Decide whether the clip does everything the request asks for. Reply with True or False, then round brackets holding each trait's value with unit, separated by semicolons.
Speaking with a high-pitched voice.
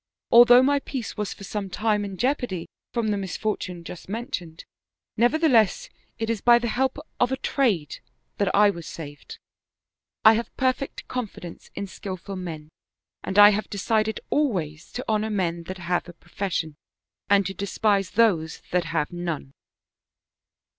True (200 Hz)